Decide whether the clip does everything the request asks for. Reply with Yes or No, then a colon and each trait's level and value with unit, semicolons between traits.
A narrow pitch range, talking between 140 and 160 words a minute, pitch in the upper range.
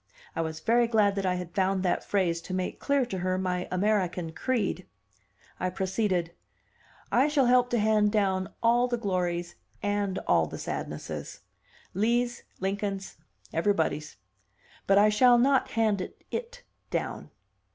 No: average, 4.2 semitones; average, 145 wpm; high, 200 Hz